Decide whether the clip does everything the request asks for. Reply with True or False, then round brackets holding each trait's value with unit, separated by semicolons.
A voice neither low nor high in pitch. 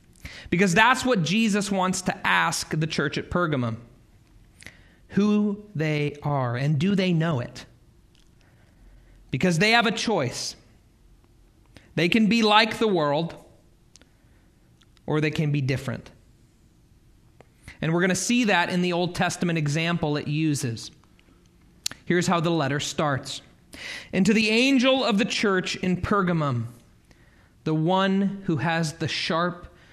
True (160 Hz)